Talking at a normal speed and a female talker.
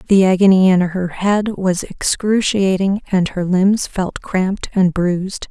Yes: average, 150 wpm; female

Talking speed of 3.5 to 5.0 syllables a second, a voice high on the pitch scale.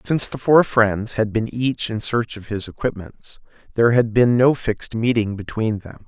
No: 4.8 syllables/s; low, 115 Hz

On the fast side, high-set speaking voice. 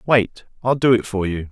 No: fast, 240 wpm; low, 110 Hz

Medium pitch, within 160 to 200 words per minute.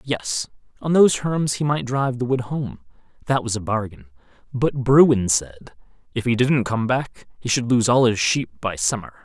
No: low, 120 Hz; average, 195 wpm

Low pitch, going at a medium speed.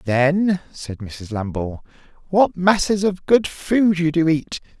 No: medium, 160 Hz; average, 150 wpm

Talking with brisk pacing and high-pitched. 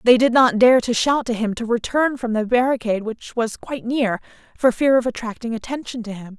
Yes: fast, 225 wpm; high, 235 Hz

